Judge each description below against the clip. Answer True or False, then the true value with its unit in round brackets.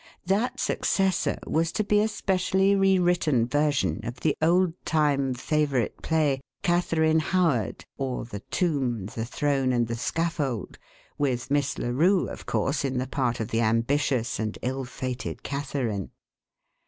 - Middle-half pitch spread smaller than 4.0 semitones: False (5.2 semitones)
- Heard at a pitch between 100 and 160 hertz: True (140 Hz)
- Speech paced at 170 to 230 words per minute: False (140 wpm)